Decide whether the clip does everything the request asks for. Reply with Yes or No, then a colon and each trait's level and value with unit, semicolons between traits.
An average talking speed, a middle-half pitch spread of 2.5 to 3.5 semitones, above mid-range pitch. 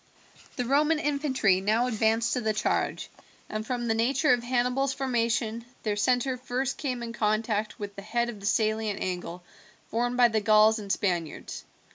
Yes: average, 170 wpm; average, 2.8 semitones; high, 230 Hz